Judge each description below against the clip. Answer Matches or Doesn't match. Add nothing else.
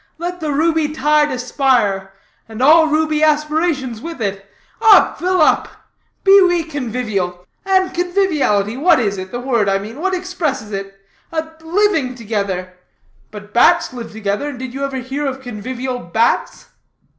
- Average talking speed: Matches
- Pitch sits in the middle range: Doesn't match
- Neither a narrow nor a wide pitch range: Doesn't match